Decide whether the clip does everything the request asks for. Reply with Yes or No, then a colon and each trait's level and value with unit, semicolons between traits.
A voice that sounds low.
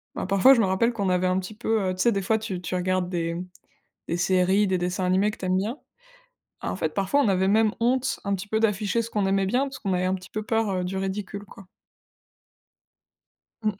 No: high, 195 Hz